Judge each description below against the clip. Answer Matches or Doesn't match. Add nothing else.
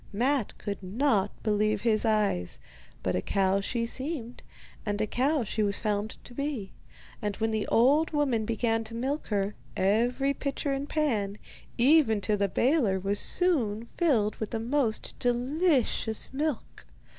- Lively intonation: Doesn't match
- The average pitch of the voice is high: Matches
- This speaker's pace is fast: Doesn't match